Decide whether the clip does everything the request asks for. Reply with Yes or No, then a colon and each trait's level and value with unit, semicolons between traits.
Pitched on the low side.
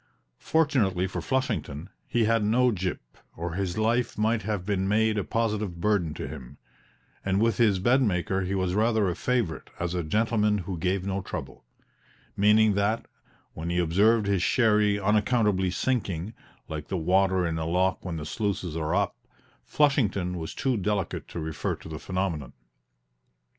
Yes: low, 100 Hz